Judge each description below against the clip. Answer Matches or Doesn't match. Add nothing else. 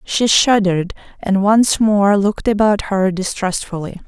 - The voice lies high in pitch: Matches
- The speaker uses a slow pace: Matches